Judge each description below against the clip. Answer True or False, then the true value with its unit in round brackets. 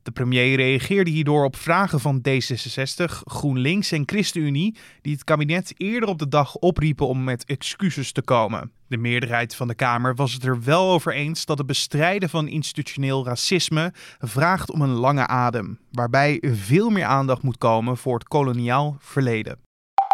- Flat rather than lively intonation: False (4.0 semitones)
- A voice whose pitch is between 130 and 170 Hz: True (140 Hz)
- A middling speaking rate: True (165 wpm)